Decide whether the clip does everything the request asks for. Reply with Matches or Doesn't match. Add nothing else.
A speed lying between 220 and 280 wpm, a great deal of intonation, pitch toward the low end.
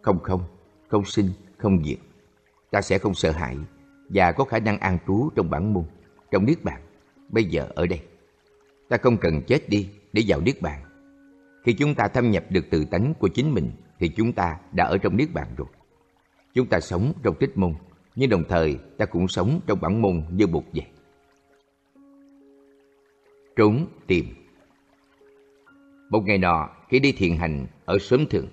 Doesn't match